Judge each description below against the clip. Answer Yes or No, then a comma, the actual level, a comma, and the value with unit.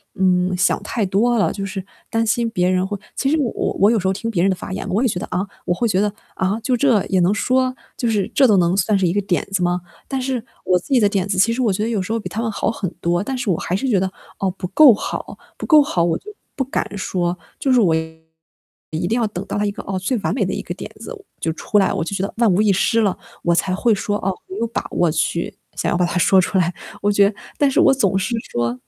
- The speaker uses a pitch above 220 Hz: No, high, 200 Hz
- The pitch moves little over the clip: No, average, 3.9 semitones